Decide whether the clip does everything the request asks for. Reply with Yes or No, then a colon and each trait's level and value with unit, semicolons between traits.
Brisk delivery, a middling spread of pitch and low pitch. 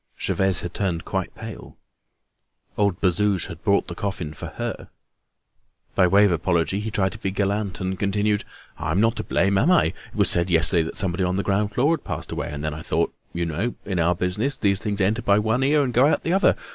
Yes: fast, 220 wpm; average, 3.2 semitones; low, 100 Hz